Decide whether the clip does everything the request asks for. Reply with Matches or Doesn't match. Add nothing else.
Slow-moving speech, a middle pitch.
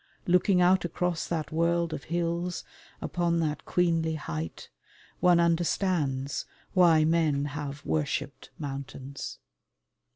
Matches